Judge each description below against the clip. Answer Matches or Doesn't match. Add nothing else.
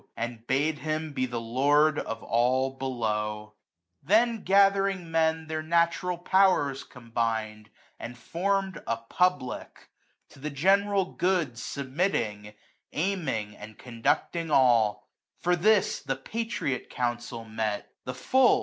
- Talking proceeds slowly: Matches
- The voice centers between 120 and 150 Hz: Matches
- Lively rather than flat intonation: Matches